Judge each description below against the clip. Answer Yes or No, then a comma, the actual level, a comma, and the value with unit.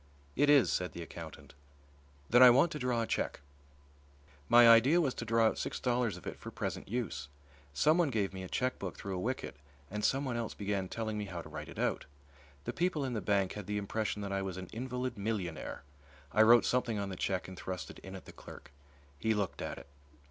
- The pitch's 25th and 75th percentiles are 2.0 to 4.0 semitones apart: No, average, 4.6 semitones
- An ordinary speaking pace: No, fast, 220 wpm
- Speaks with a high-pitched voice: No, low, 110 Hz